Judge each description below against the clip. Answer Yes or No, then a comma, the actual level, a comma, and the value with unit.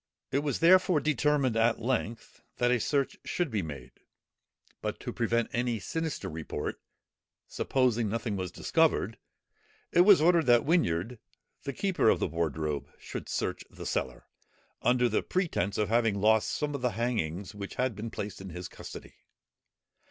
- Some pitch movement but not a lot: No, wide, 6.1 semitones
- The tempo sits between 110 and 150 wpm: No, average, 160 wpm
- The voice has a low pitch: Yes, low, 115 Hz